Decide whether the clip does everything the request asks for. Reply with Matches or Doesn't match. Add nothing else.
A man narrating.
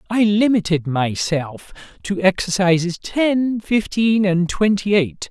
Matches